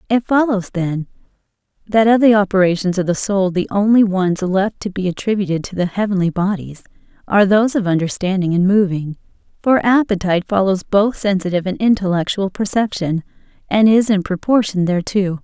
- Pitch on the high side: Yes, high, 195 Hz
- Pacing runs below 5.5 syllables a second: No, 5.6 syllables/s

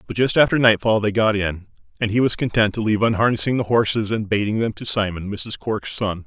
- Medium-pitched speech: No, low, 110 Hz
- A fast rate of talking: Yes, fast, 230 wpm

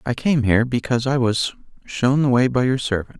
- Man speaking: Yes, male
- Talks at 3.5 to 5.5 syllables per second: No, 5.7 syllables/s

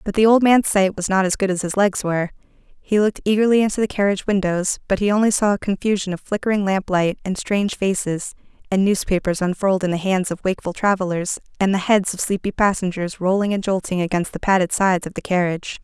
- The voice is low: No, high, 195 Hz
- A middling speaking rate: No, fast, 215 wpm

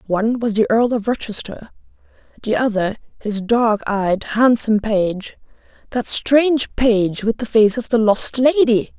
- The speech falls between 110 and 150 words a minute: Yes, average, 145 wpm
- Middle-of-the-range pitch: No, high, 230 Hz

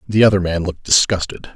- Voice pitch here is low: Yes, very low, 95 Hz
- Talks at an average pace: Yes, average, 195 wpm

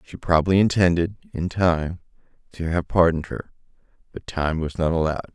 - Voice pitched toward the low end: Yes, very low, 85 Hz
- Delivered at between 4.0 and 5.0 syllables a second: No, 5.8 syllables/s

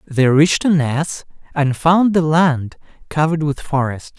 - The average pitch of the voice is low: No, medium, 150 Hz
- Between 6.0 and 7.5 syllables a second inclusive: No, 4.4 syllables/s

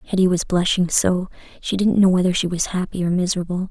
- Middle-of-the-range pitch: Yes, medium, 180 Hz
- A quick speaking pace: Yes, fast, 210 wpm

